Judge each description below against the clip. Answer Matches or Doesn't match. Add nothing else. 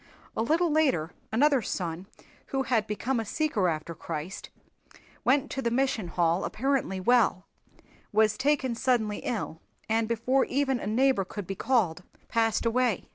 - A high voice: Matches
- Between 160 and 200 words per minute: Doesn't match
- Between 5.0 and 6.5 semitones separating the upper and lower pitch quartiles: Matches